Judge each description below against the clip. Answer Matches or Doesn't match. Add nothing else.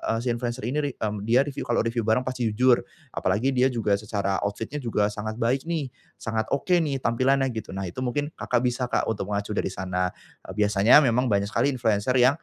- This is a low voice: Matches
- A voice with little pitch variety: Doesn't match